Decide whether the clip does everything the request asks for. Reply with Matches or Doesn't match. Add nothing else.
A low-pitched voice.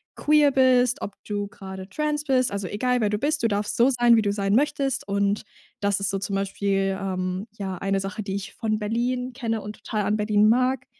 Doesn't match